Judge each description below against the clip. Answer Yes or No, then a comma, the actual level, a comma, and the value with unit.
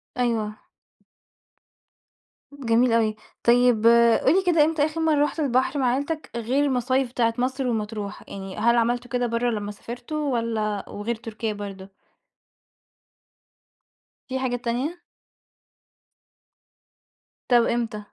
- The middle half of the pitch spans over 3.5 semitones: No, average, 2.8 semitones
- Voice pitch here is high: Yes, high, 240 Hz